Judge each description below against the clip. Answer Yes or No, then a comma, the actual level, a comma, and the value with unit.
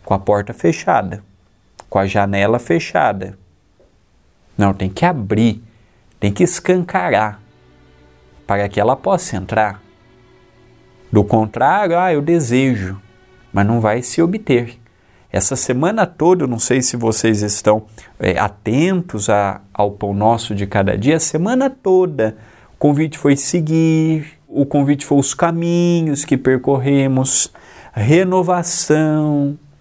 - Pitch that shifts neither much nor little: No, wide, 7.0 semitones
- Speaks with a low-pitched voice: Yes, low, 120 Hz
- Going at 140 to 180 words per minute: No, average, 125 wpm